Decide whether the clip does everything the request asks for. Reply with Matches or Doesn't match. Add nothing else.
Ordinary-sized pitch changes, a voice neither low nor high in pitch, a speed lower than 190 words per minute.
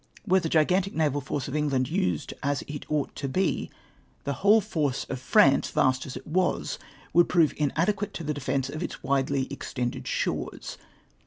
Matches